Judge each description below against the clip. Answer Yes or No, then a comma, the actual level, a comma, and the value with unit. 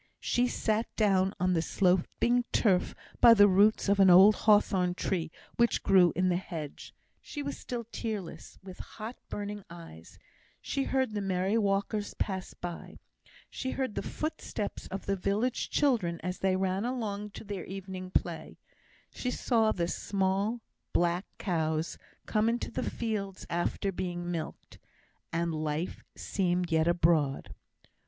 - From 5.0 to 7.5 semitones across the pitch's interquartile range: No, average, 3.5 semitones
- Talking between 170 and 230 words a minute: No, average, 145 wpm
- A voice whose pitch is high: Yes, high, 195 Hz